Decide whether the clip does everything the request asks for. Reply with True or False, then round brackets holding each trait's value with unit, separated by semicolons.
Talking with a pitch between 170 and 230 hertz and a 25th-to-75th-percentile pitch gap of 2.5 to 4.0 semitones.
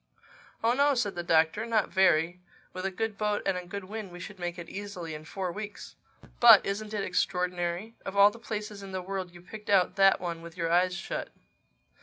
True (190 Hz; 3.0 semitones)